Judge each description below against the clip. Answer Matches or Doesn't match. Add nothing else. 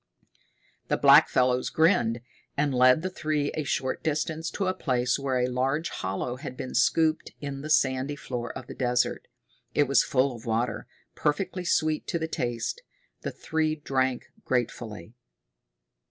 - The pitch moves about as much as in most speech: Matches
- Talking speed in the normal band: Matches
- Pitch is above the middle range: Doesn't match